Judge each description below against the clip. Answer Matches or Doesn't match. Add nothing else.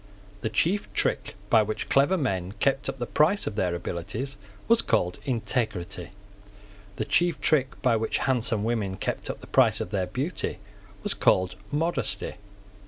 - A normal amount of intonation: Doesn't match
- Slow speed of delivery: Doesn't match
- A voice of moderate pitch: Doesn't match